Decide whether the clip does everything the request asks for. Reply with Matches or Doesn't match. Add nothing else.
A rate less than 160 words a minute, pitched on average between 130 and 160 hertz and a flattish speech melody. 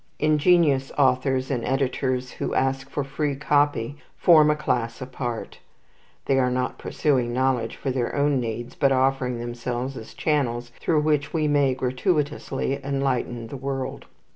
Matches